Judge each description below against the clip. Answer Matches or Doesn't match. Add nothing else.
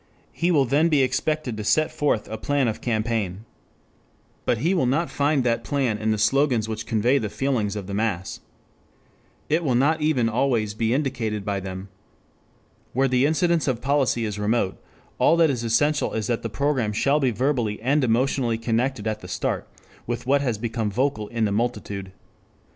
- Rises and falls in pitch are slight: Doesn't match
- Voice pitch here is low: Matches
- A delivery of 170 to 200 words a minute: Matches